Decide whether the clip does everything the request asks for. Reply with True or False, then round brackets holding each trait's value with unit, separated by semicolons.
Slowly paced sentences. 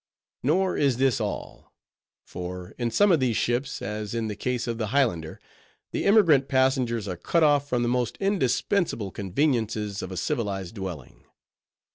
False (160 wpm)